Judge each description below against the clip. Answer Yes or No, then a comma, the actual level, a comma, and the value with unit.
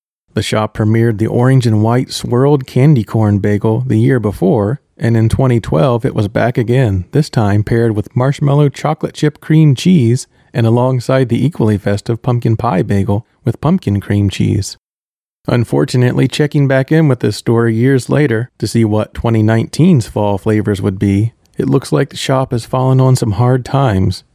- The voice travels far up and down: No, average, 3.5 semitones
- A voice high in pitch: No, low, 120 Hz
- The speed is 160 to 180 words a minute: Yes, average, 175 wpm